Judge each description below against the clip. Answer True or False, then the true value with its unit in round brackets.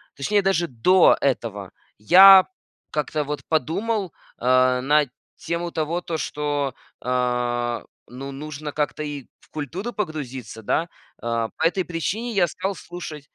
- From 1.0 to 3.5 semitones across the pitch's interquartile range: False (5.4 semitones)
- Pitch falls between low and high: True (150 Hz)